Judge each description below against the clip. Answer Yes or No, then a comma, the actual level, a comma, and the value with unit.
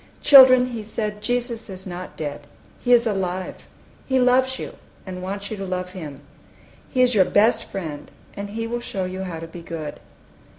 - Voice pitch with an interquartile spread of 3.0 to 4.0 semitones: No, average, 4.8 semitones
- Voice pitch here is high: Yes, high, 200 Hz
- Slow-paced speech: No, average, 185 wpm